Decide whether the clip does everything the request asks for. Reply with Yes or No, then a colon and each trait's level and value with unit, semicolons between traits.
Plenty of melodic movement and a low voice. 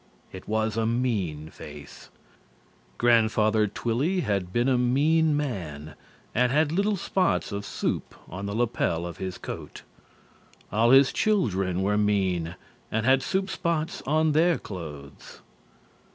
Yes: wide, 7.5 semitones; low, 110 Hz